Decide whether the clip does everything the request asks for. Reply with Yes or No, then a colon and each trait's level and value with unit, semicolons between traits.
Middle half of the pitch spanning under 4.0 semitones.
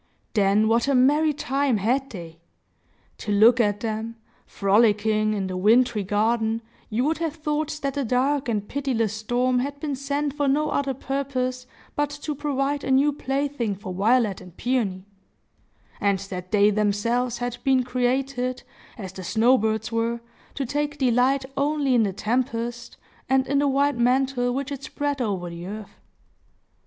No: average, 4.4 semitones